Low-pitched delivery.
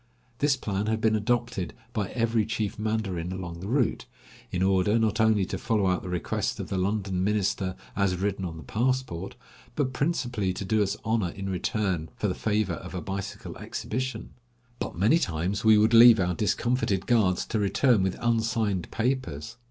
Yes: low, 105 Hz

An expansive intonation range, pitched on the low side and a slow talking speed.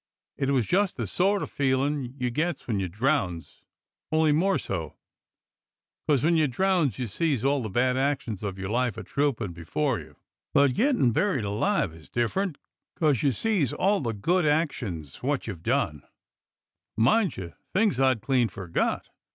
No: wide, 6.5 semitones; low, 130 Hz; average, 165 wpm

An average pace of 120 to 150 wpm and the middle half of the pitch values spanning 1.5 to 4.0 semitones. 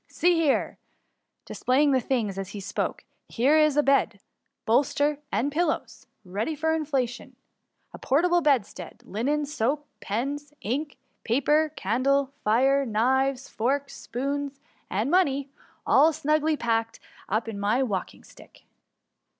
No: slow, 135 wpm; average, 4.4 semitones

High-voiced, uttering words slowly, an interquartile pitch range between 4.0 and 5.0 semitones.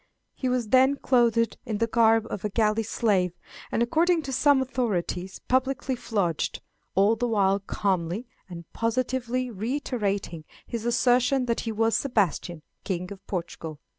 No: high, 225 Hz; average, 145 wpm; average, 4.3 semitones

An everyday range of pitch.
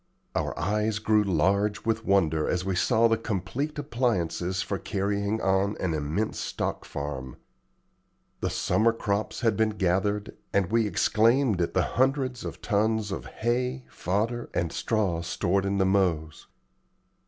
Yes: average, 3.6 semitones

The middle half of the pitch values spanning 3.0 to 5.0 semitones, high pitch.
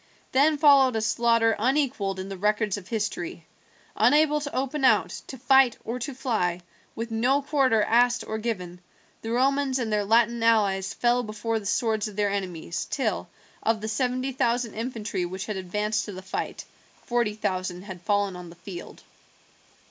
Yes: average, 4.0 semitones; high, 225 Hz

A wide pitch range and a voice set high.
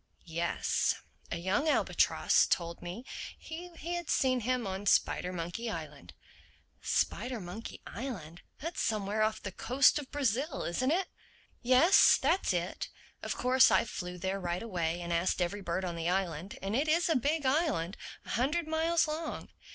Yes: wide, 8.1 semitones; high, 215 Hz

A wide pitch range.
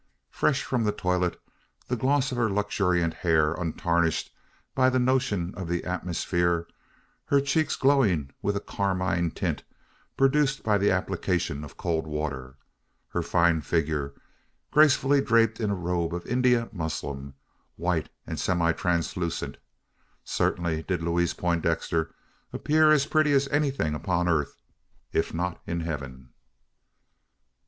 Yes: wide, 6.2 semitones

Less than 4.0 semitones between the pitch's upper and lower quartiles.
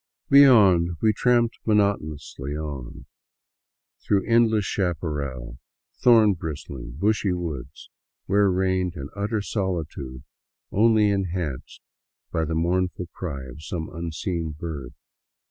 No: average, 5.3 semitones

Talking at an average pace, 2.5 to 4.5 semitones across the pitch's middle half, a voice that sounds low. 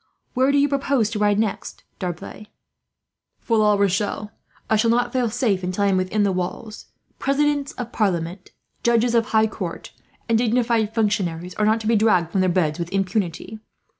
No: average, 180 wpm; average, 3.9 semitones; high, 215 Hz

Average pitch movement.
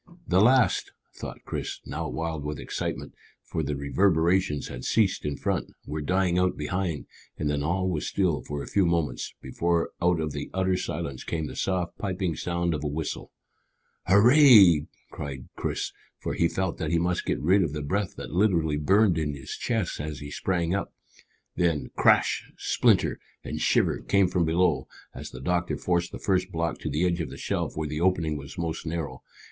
Yes: average, 3.6 semitones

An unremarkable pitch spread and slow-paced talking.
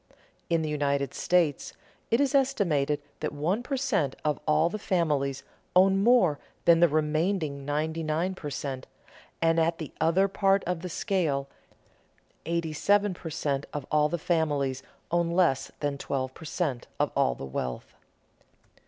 No: average, 3.9 semitones; average, 160 wpm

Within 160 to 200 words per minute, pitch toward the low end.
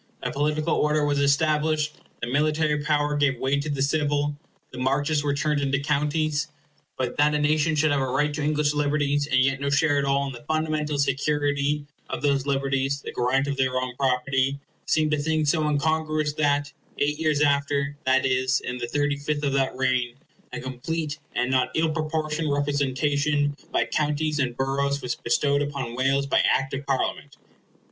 No: average, 180 wpm; medium, 145 Hz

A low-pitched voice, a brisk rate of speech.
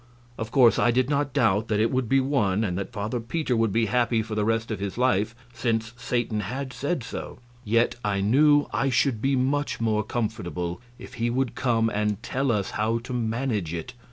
Yes: low, 115 Hz; fast, 210 wpm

